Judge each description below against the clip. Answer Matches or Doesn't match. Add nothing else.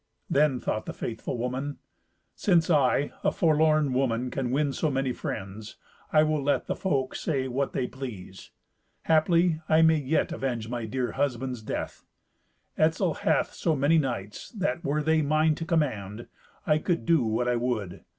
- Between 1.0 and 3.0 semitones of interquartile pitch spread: Doesn't match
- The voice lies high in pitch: Doesn't match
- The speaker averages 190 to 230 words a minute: Doesn't match